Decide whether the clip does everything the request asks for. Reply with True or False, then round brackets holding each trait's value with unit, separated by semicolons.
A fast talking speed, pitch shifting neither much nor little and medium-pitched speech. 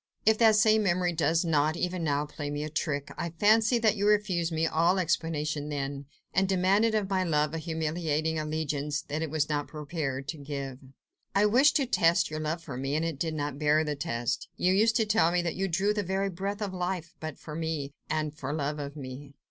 True (220 wpm; 4.2 semitones; 160 Hz)